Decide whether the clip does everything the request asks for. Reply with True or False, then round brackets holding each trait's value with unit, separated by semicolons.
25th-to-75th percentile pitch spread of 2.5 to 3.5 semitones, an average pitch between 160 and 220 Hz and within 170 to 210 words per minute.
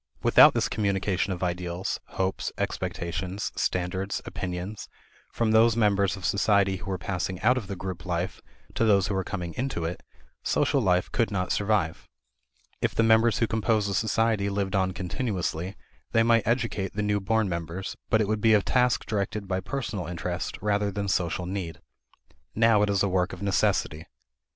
False (2.9 semitones; 100 Hz; 175 wpm)